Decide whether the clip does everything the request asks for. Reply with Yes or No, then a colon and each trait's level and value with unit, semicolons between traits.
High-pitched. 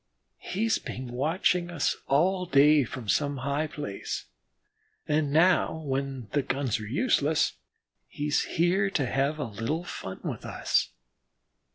No: medium, 145 Hz